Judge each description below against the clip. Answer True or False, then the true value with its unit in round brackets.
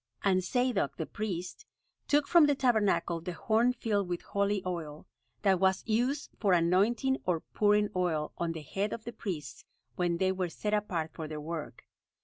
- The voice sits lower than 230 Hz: True (190 Hz)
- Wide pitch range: False (4.3 semitones)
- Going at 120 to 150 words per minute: False (175 wpm)